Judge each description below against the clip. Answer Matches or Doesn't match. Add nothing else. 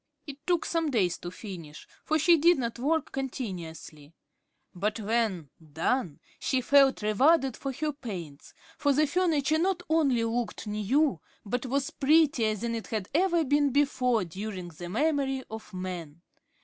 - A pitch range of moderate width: Doesn't match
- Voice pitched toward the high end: Matches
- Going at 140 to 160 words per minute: Matches